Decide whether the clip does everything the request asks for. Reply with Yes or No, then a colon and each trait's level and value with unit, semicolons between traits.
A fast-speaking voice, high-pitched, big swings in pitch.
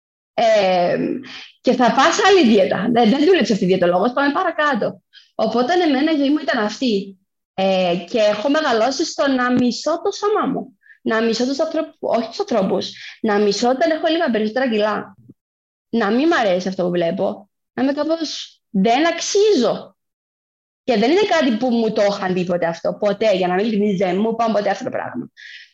Yes: fast, 180 wpm; high, 235 Hz; wide, 7.4 semitones